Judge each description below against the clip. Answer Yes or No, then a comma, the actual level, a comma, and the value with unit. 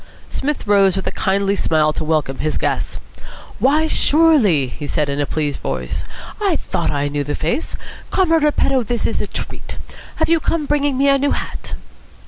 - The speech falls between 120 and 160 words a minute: No, average, 185 wpm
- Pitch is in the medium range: No, high, 205 Hz